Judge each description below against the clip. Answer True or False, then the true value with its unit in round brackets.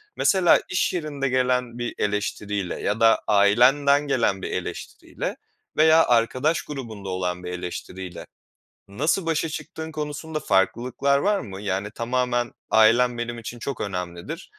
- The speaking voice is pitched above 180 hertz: False (120 Hz)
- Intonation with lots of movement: True (6.2 semitones)